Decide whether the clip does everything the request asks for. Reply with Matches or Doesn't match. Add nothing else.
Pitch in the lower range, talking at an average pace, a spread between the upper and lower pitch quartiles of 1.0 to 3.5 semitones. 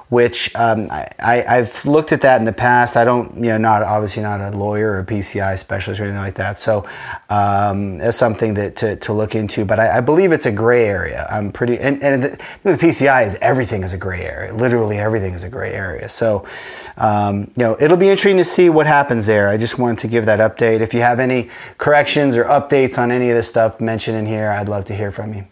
Doesn't match